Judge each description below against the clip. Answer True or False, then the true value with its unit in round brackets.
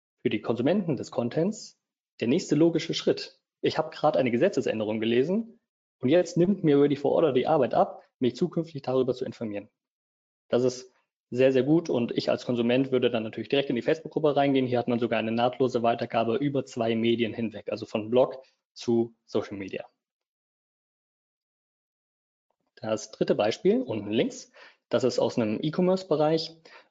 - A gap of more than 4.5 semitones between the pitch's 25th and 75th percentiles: True (4.9 semitones)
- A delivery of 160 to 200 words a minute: True (165 wpm)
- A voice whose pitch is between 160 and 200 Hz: False (125 Hz)